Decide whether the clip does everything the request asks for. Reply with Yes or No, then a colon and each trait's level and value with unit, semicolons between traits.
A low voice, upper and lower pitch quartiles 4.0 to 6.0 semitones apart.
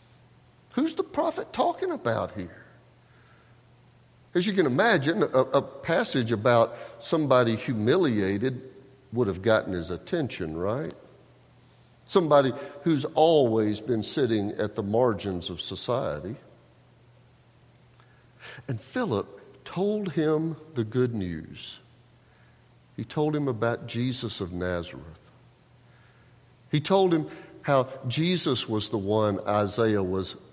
Yes: low, 125 Hz; average, 4.8 semitones